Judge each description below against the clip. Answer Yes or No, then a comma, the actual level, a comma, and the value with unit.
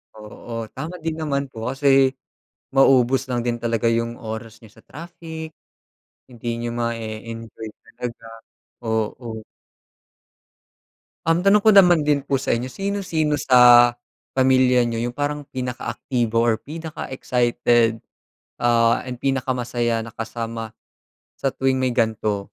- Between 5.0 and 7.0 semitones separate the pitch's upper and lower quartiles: No, average, 3.1 semitones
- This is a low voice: Yes, low, 120 Hz